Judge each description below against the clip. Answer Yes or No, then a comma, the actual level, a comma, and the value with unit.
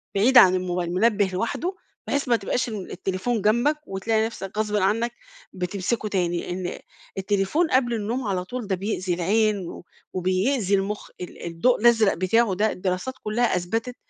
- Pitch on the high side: Yes, high, 205 Hz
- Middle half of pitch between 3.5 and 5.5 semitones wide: Yes, average, 4.0 semitones